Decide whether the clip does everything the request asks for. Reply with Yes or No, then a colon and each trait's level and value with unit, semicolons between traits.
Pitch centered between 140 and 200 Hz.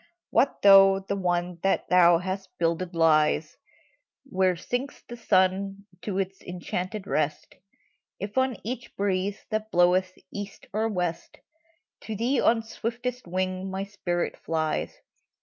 Yes: high, 190 Hz